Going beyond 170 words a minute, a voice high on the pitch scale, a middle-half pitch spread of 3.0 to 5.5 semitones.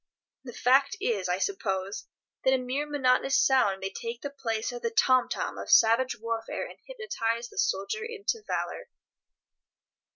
No: average, 160 wpm; high, 245 Hz; average, 3.5 semitones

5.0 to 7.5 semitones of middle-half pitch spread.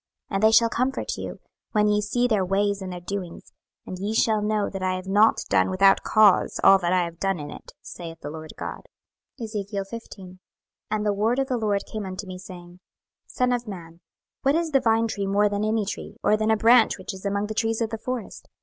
No: average, 2.9 semitones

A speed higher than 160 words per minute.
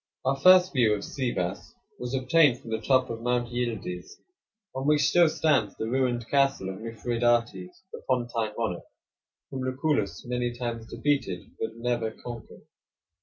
No: average, 150 wpm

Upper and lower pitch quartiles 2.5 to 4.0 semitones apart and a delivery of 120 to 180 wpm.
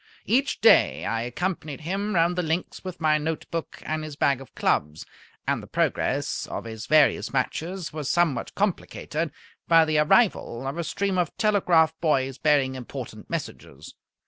No: average, 4.6 semitones; average, 165 wpm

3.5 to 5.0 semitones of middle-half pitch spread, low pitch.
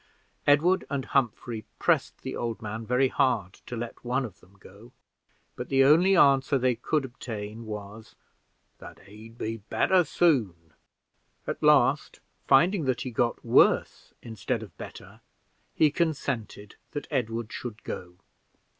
Yes: average, 4.1 semitones; low, 120 Hz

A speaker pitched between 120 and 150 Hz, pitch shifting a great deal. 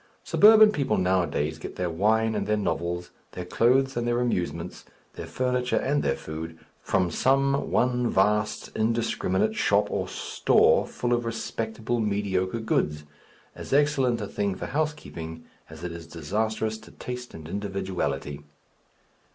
No: low, 105 Hz; wide, 5.7 semitones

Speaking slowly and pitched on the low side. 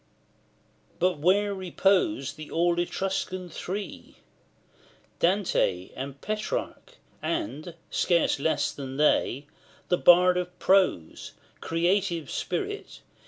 No: slow, 100 wpm; medium, 180 Hz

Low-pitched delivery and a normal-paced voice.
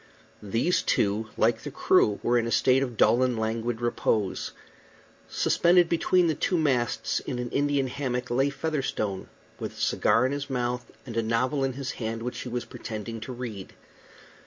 Yes: low, 125 Hz; average, 180 wpm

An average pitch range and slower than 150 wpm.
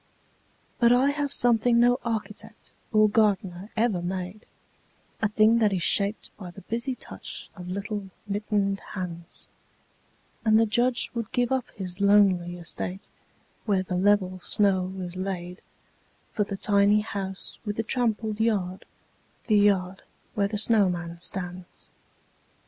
Yes: average, 3.1 semitones; average, 140 wpm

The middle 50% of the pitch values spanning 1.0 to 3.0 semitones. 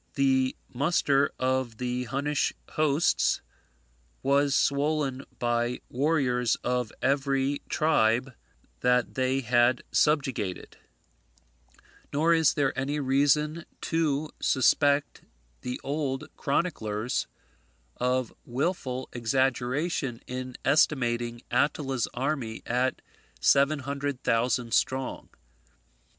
Yes: narrow, 2.5 semitones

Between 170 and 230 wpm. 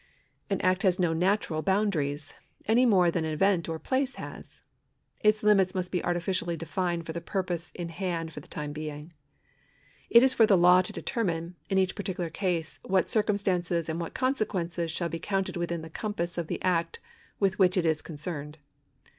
Yes: average, 190 wpm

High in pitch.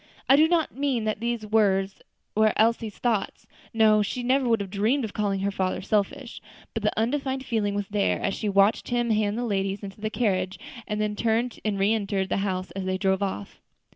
Yes: high, 215 Hz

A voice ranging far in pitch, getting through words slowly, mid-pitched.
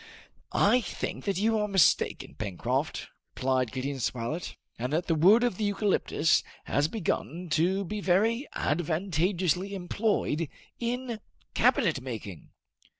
Yes: wide, 6.0 semitones; slow, 125 wpm; medium, 180 Hz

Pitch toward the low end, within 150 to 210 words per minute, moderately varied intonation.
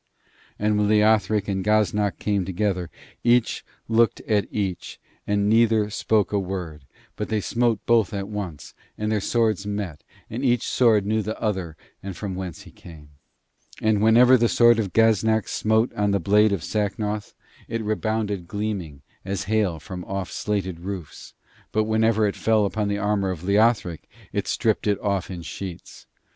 No: low, 105 Hz; average, 165 wpm; narrow, 2.3 semitones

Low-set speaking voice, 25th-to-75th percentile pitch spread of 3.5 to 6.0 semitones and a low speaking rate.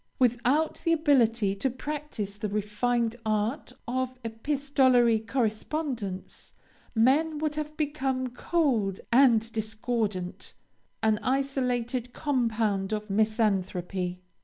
No: high, 235 Hz; average, 4.1 semitones; slow, 90 wpm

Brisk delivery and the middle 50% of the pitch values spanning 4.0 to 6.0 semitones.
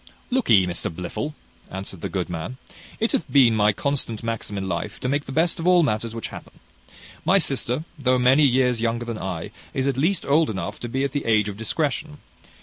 Yes: fast, 210 wpm; wide, 5.4 semitones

